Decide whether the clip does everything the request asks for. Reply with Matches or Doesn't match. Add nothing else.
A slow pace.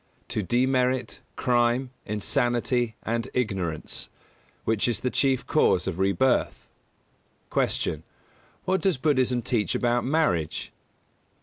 Matches